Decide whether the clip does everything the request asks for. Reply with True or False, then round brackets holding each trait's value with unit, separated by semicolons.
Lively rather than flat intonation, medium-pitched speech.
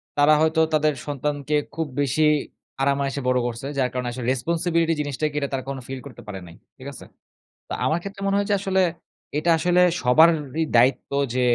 False (3.7 semitones; 145 Hz)